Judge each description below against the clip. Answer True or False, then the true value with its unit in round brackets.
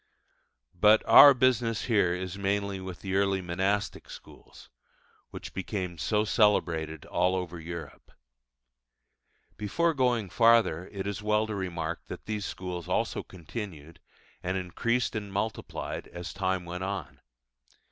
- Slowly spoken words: True (130 wpm)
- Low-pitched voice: True (95 Hz)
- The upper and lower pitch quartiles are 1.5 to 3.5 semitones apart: True (3.2 semitones)